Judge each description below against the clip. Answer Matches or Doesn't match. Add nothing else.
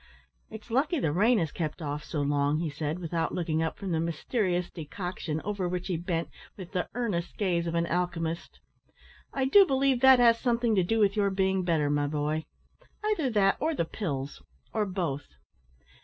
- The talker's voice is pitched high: Doesn't match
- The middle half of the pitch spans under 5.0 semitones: Doesn't match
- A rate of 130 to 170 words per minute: Doesn't match